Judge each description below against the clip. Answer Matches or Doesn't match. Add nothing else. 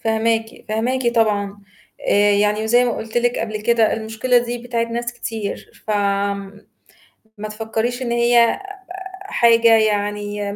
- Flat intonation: Matches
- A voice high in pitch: Matches